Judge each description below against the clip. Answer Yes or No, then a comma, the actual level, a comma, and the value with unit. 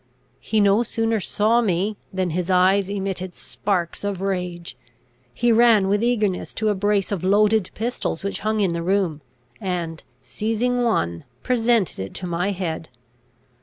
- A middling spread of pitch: Yes, average, 3.3 semitones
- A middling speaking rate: Yes, average, 155 wpm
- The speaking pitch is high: Yes, high, 195 Hz